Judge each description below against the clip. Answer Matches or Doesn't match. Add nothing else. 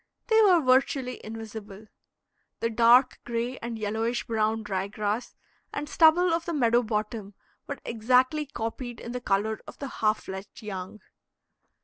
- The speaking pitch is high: Matches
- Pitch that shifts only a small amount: Doesn't match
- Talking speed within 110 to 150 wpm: Matches